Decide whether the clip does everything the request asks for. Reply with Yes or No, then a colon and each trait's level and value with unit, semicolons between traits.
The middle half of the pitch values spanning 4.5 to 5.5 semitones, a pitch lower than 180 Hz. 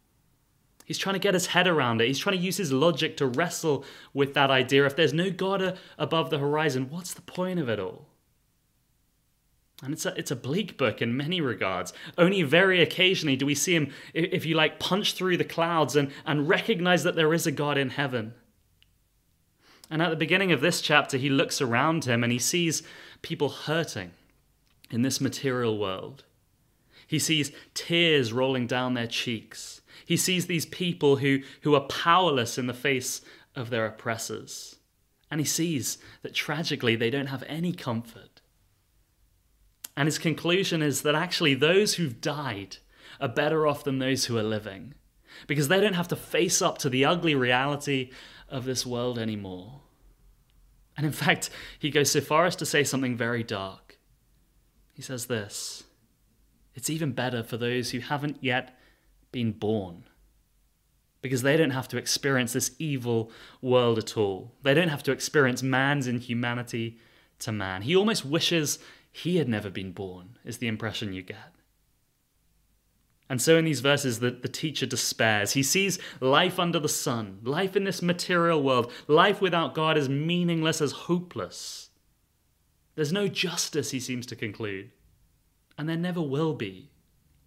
Yes: average, 4.9 semitones; medium, 140 Hz